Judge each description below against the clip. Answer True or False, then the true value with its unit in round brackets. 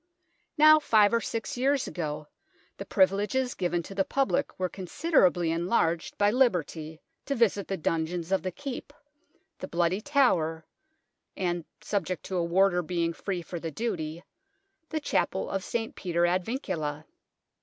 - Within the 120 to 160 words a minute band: True (155 wpm)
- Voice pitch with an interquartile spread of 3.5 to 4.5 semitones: False (5.4 semitones)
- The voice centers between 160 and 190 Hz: True (185 Hz)